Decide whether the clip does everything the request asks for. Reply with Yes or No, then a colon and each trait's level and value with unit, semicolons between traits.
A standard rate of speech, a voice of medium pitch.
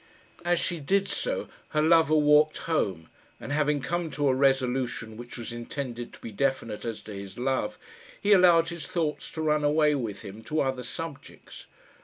Yes: average, 180 wpm; medium, 145 Hz